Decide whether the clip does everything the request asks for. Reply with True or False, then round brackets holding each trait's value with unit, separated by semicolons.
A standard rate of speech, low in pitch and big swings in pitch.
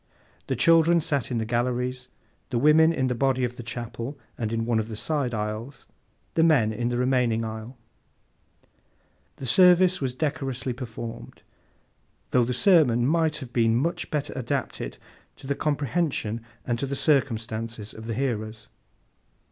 False (155 wpm; 125 Hz; 3.8 semitones)